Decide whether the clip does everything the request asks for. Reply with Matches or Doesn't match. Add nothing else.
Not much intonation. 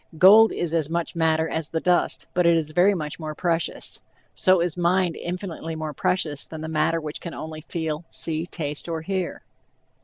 Matches